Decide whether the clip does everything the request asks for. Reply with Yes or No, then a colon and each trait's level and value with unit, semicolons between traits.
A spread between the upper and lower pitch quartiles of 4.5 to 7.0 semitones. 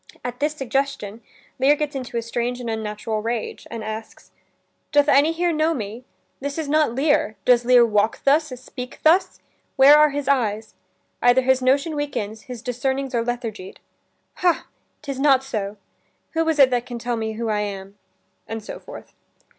No: average, 4.1 semitones